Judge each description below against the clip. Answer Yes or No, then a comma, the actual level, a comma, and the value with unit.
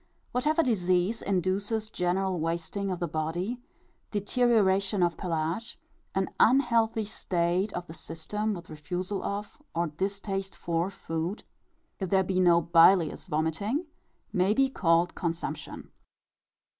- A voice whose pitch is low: No, medium, 185 Hz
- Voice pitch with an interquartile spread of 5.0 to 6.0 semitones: No, average, 3.6 semitones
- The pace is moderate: No, slow, 120 wpm